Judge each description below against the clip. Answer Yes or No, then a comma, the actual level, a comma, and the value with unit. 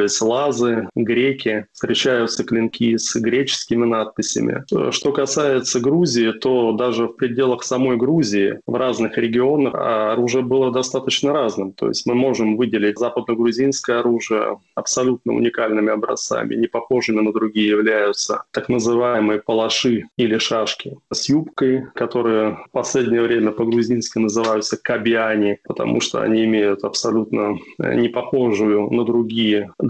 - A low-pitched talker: Yes, low, 115 Hz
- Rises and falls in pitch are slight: Yes, narrow, 2.1 semitones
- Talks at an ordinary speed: Yes, average, 120 wpm